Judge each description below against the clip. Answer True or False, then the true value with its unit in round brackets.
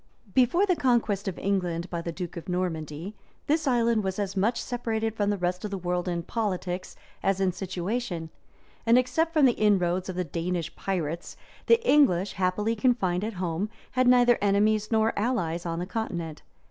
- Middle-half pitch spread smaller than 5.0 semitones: True (4.5 semitones)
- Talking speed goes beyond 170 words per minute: True (180 wpm)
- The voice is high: True (195 Hz)